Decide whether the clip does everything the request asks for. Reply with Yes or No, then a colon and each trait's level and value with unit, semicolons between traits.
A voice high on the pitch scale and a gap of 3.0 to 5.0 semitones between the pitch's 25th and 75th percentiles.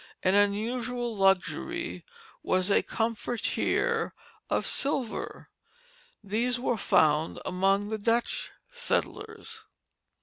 Yes: high, 225 Hz; average, 4.0 semitones